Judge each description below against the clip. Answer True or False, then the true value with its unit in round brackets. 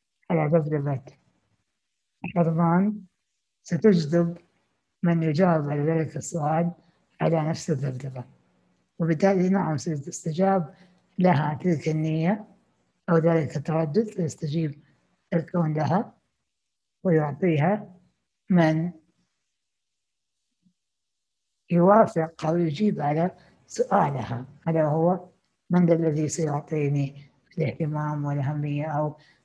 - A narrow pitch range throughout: False (3.0 semitones)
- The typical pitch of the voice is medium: True (160 Hz)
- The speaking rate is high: False (80 wpm)